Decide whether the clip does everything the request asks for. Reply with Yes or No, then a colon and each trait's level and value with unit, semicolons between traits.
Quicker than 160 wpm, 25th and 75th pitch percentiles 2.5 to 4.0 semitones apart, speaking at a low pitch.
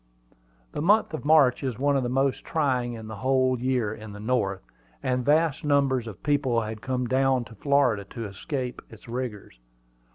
Yes: average, 185 wpm; average, 3.4 semitones; low, 125 Hz